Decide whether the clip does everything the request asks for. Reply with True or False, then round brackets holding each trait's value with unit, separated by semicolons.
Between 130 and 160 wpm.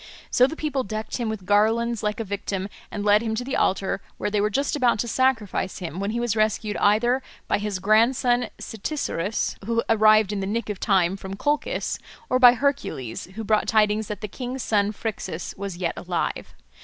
False (200 wpm)